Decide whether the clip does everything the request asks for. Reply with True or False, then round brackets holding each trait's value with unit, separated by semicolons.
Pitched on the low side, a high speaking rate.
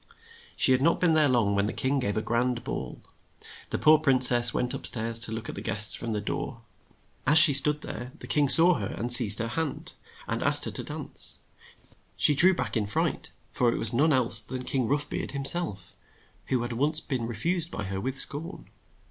True (125 Hz; 225 wpm)